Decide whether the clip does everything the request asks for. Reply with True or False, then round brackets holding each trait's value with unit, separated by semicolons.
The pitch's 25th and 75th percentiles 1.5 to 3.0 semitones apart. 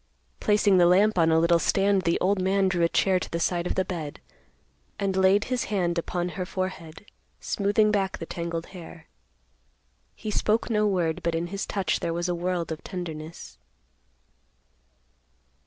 True (2.7 semitones)